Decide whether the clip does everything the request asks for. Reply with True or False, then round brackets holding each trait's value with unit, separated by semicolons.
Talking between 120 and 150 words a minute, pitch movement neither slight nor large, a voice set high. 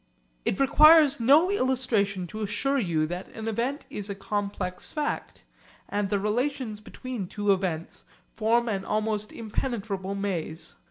True (140 wpm; 4.5 semitones; 210 Hz)